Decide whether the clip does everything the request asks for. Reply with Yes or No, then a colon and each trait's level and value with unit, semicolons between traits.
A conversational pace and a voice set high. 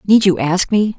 No: fast, 245 wpm; high, 195 Hz